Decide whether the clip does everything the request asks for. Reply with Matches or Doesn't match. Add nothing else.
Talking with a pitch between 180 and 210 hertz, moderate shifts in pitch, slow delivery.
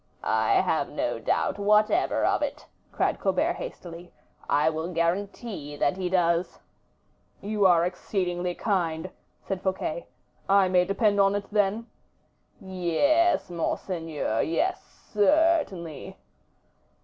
Matches